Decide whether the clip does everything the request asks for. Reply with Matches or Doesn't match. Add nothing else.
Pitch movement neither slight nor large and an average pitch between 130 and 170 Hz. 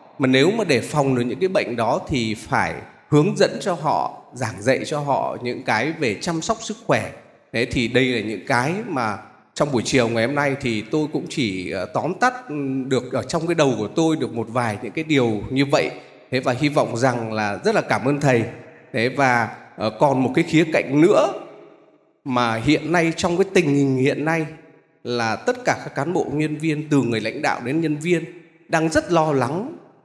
Matches